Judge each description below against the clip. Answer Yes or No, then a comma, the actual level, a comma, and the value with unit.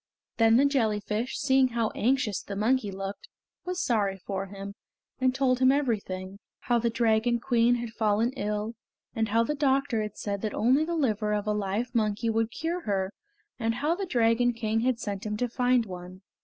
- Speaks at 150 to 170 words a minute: No, average, 185 wpm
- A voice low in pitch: No, high, 225 Hz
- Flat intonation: No, average, 3.3 semitones